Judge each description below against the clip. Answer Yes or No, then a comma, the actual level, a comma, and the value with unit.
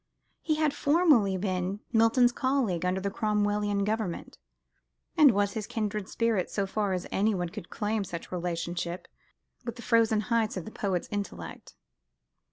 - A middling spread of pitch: Yes, average, 3.4 semitones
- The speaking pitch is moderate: No, high, 205 Hz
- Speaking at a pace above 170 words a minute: No, average, 150 wpm